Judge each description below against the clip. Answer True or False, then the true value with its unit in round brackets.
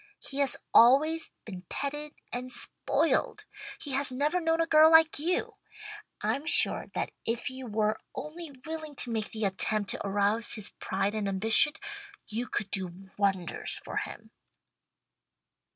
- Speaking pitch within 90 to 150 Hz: False (245 Hz)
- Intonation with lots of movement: True (6.5 semitones)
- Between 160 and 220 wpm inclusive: False (150 wpm)